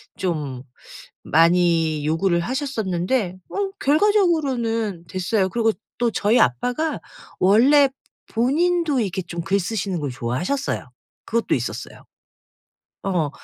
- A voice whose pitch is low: No, high, 200 Hz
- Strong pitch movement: Yes, wide, 7.5 semitones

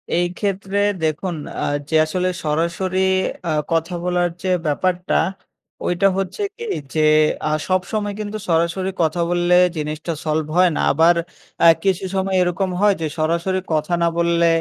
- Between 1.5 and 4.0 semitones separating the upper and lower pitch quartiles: Yes, narrow, 2.4 semitones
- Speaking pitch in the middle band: Yes, medium, 175 Hz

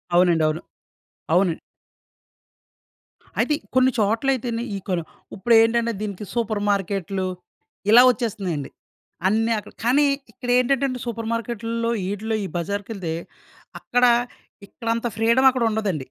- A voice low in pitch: No, high, 225 Hz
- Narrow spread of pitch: No, average, 3.4 semitones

